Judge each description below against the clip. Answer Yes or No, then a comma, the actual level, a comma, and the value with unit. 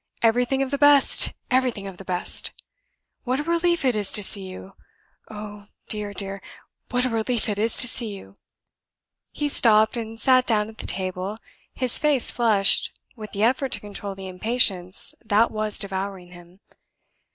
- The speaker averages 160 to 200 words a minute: Yes, average, 170 wpm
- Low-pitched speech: No, high, 215 Hz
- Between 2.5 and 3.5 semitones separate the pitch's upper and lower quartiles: No, average, 4.1 semitones